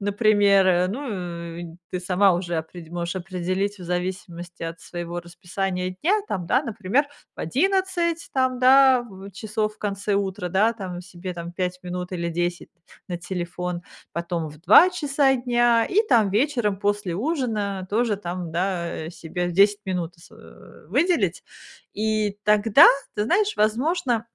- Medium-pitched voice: No, high, 195 Hz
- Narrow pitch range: No, average, 4.4 semitones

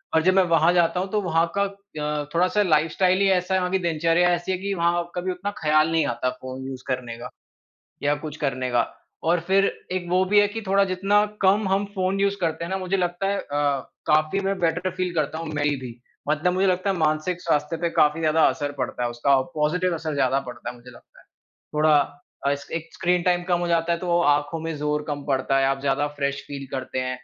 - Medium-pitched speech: Yes, medium, 165 Hz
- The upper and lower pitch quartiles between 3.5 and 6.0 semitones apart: Yes, average, 4.0 semitones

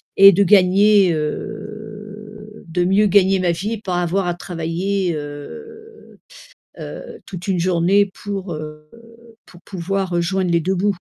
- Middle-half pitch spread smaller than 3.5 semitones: Yes, average, 2.9 semitones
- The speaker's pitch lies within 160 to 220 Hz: Yes, high, 190 Hz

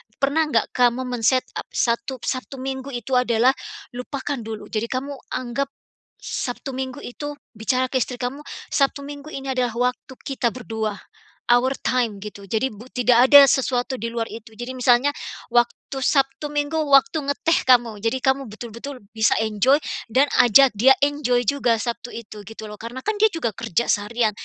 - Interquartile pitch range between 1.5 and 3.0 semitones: Yes, average, 2.7 semitones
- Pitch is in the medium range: No, very high, 250 Hz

